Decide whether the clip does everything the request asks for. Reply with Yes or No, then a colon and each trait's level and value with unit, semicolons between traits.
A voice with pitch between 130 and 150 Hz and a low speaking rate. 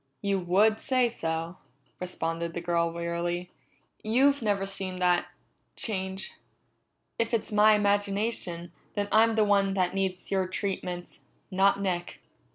No: high, 195 Hz; slow, 130 wpm